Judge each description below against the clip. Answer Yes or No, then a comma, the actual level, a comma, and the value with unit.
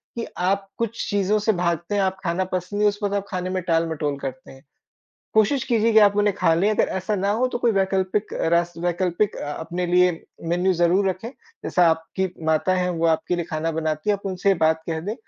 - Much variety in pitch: No, average, 3.4 semitones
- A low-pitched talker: No, medium, 185 Hz